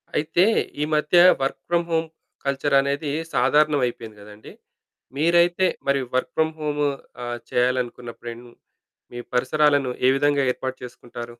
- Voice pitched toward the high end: No, medium, 140 Hz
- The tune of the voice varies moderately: Yes, average, 3.6 semitones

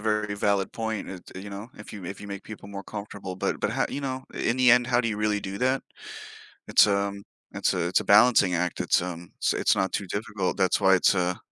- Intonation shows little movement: Yes, narrow, 2.3 semitones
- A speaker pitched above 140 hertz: No, low, 100 Hz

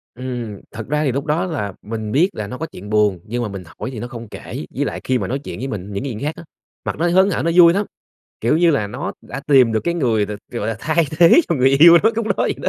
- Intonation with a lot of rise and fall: Yes, wide, 6.9 semitones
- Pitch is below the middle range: Yes, low, 130 Hz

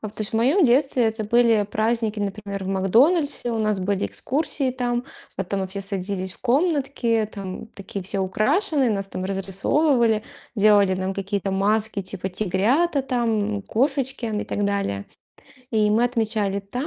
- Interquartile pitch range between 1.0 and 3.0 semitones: No, average, 3.7 semitones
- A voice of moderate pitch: No, high, 215 Hz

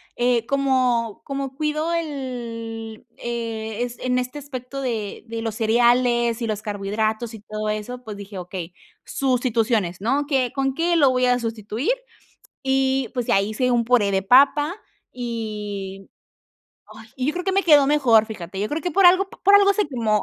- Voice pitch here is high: Yes, high, 240 Hz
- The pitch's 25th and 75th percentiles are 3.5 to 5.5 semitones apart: Yes, average, 3.8 semitones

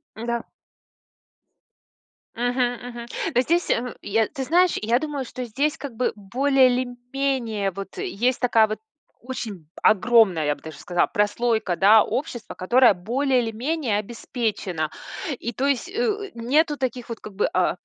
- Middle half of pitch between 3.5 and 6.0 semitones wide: Yes, average, 3.8 semitones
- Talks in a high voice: Yes, high, 240 Hz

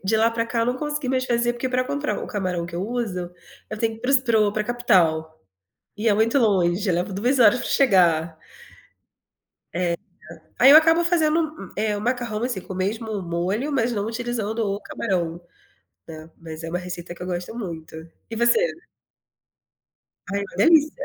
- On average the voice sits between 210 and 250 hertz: Yes, high, 215 Hz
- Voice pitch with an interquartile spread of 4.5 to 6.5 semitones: Yes, average, 5.3 semitones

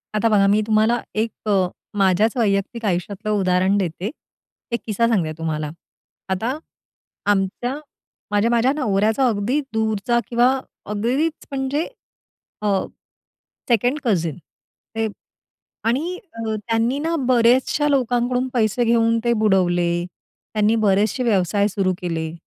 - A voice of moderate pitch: No, high, 220 Hz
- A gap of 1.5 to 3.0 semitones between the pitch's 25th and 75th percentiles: No, average, 3.5 semitones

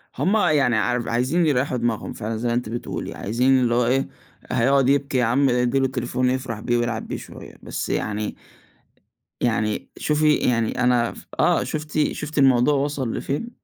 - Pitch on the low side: Yes, low, 125 Hz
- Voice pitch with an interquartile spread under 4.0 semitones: Yes, average, 2.8 semitones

